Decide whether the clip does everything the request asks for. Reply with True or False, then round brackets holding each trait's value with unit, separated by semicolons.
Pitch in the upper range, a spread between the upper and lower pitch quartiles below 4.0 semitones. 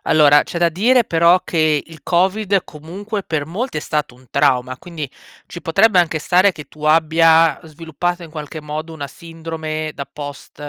False (160 Hz; 2.6 semitones)